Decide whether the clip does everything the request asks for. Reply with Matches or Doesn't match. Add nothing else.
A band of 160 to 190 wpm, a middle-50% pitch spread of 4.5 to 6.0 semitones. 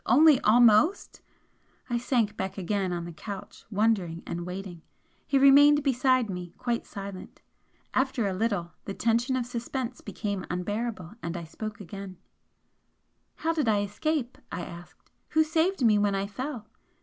Doesn't match